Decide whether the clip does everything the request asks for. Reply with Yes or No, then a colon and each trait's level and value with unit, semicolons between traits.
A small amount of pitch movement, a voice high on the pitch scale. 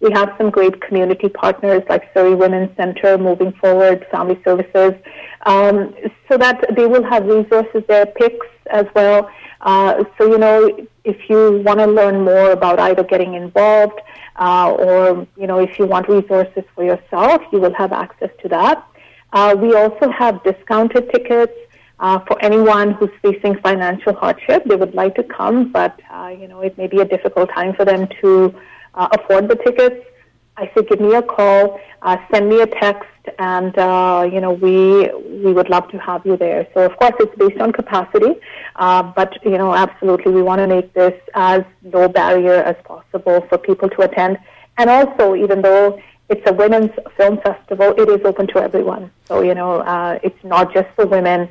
Yes: narrow, 2.2 semitones; high, 195 Hz